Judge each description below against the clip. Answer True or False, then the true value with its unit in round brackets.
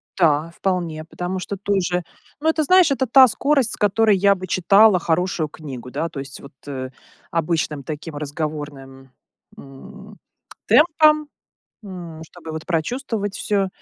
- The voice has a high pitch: False (180 Hz)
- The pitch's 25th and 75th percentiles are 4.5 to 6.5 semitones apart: True (5.1 semitones)